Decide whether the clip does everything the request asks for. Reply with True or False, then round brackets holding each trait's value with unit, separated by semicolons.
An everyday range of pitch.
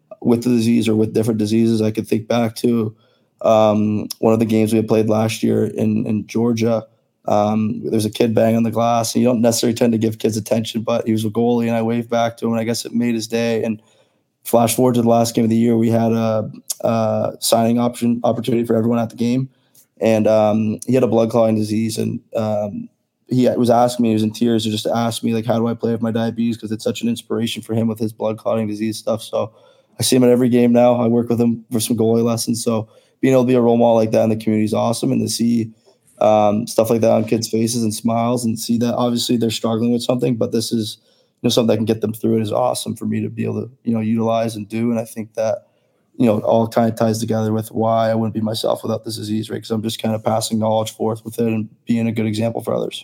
False (1.1 semitones)